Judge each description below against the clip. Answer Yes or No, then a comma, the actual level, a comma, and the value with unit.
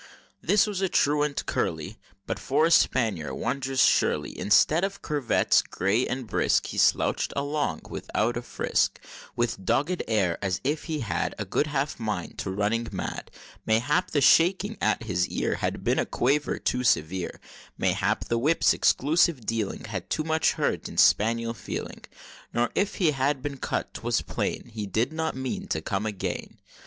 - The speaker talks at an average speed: Yes, average, 170 wpm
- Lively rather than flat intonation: Yes, wide, 5.7 semitones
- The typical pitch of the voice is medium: No, low, 125 Hz